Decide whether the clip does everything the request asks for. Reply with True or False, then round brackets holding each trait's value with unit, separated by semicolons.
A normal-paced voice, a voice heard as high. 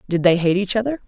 False (280 wpm; 200 Hz)